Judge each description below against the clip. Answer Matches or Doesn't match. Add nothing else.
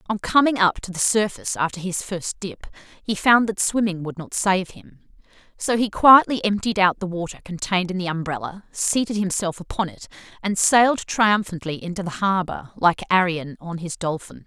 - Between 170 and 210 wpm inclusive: Matches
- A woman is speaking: Matches